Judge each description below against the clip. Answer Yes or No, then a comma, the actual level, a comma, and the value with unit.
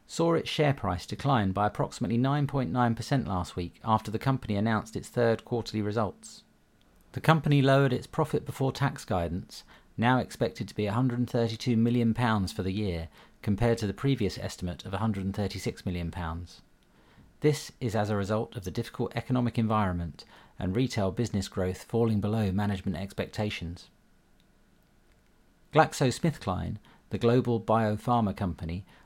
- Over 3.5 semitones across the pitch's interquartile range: Yes, average, 4.3 semitones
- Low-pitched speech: Yes, low, 110 Hz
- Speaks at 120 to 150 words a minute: Yes, slow, 135 wpm